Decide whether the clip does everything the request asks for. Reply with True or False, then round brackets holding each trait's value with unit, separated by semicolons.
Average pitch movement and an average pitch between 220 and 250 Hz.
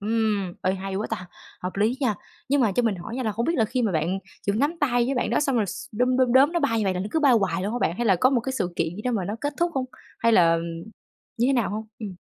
True (4.8 semitones; 225 Hz)